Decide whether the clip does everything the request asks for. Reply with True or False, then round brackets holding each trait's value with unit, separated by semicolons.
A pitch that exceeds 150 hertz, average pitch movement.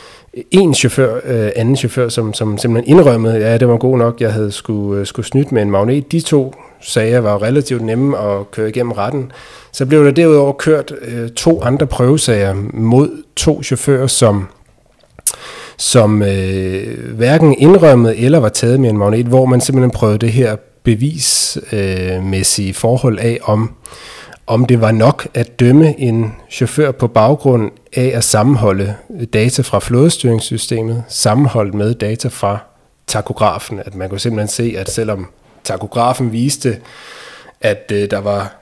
False (120 Hz; 3.7 semitones)